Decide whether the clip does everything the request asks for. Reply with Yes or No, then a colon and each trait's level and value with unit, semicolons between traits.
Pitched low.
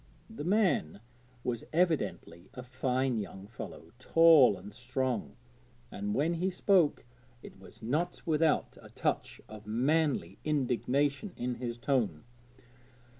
Yes: low, 130 Hz